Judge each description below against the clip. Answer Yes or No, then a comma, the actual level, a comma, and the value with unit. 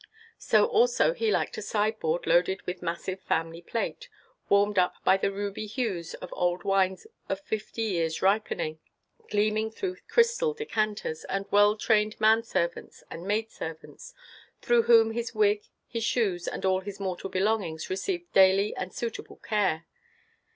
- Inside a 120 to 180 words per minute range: Yes, average, 150 wpm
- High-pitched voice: Yes, high, 205 Hz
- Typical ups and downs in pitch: Yes, average, 3.3 semitones